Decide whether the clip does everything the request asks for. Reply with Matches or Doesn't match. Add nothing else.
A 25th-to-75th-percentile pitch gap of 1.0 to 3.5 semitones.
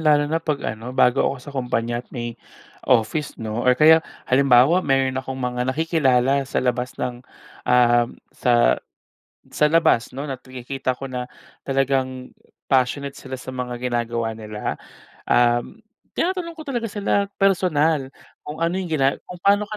Doesn't match